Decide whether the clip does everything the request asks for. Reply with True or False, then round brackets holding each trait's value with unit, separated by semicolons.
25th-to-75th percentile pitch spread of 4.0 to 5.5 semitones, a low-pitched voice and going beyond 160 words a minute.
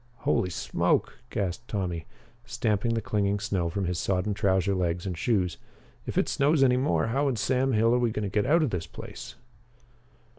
True (4.8 semitones; 105 Hz; 190 wpm)